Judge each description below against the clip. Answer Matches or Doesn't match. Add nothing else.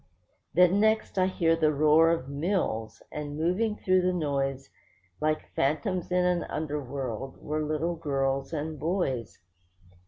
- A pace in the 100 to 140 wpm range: Matches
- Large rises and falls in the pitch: Doesn't match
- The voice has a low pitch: Doesn't match